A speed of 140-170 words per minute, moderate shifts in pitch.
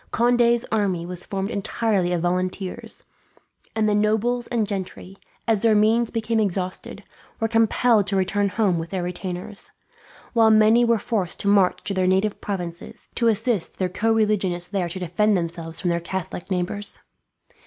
Yes: average, 165 wpm; average, 3.4 semitones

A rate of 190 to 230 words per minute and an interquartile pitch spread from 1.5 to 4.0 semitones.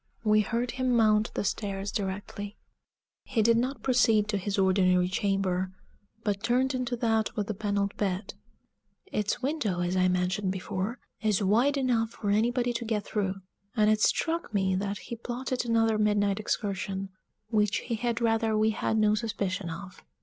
No: average, 165 wpm; average, 3.0 semitones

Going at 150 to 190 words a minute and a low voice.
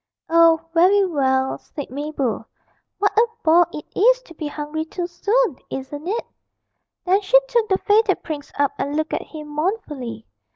No: average, 165 wpm; very high, 325 Hz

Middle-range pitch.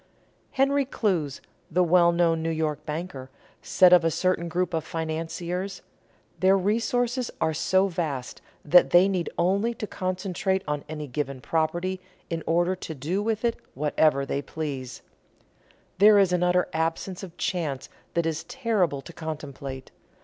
Yes: medium, 170 Hz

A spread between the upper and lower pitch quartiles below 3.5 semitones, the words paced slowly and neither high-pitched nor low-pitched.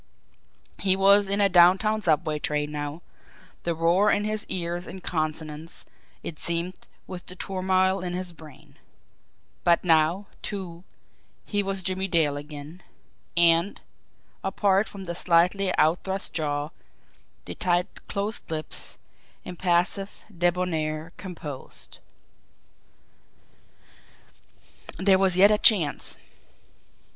Yes: average, 3.1 semitones; slow, 110 wpm; medium, 180 Hz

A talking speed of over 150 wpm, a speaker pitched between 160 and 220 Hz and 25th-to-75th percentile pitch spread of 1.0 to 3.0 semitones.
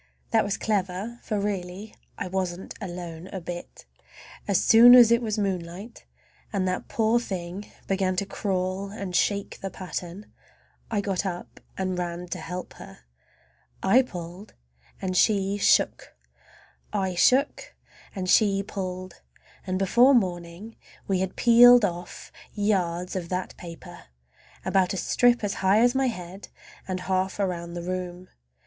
No: average, 145 wpm; high, 190 Hz; narrow, 2.5 semitones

